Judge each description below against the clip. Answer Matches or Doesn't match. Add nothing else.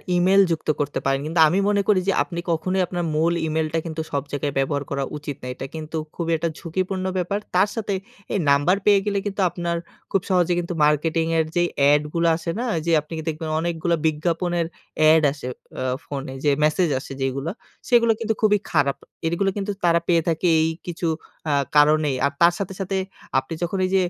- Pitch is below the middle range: Doesn't match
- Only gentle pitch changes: Doesn't match